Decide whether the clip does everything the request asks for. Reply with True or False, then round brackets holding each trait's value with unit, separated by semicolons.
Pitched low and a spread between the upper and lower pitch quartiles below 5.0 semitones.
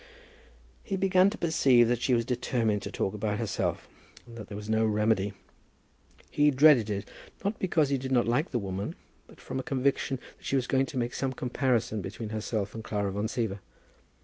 True (120 Hz; 4.0 semitones)